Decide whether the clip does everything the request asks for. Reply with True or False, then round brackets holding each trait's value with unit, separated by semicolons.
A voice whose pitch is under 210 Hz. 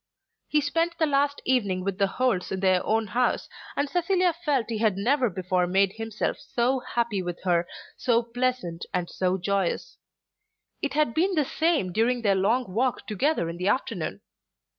False (230 Hz)